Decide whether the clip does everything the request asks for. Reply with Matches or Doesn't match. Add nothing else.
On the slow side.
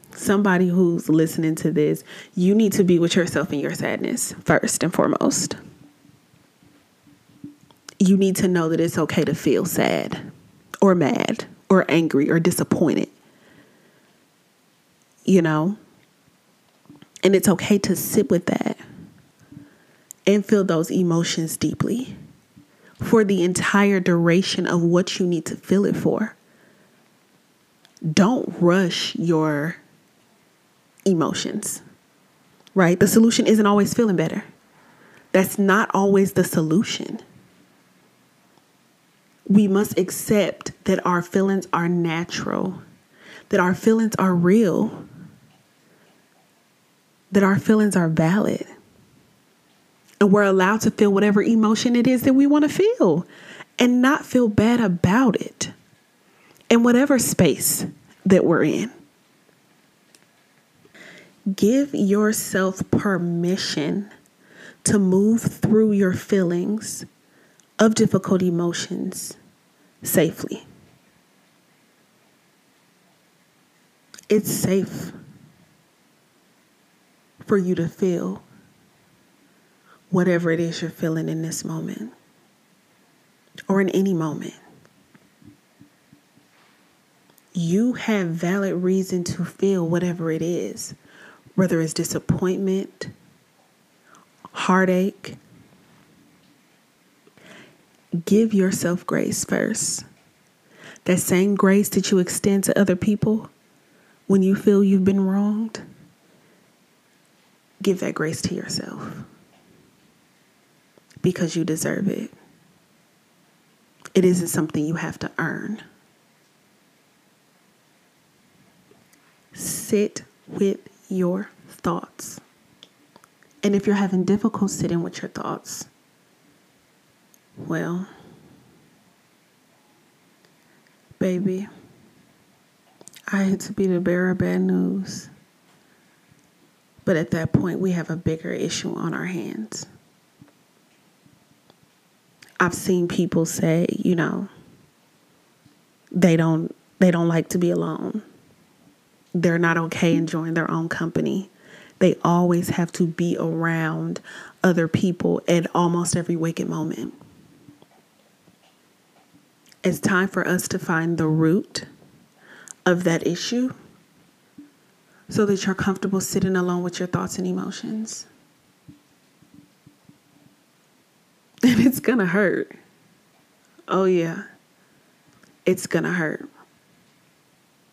Matches